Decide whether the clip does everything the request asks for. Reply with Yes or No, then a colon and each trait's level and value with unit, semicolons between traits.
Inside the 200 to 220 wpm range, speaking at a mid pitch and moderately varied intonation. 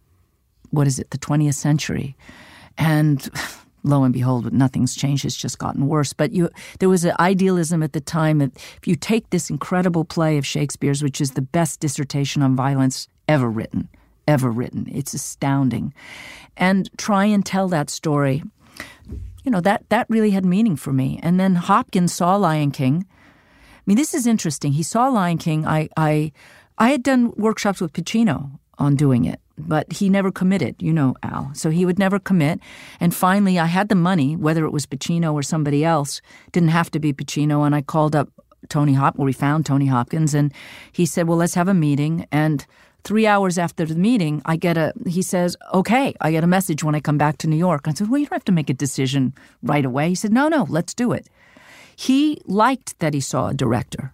Yes: fast, 205 wpm; medium, 160 Hz; average, 4.6 semitones